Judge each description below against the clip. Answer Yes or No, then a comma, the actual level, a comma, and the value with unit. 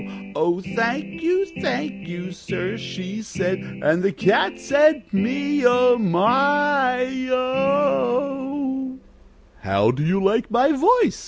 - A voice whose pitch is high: Yes, very high, 250 Hz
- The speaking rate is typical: No, slow, 115 wpm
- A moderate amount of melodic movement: No, wide, 6.3 semitones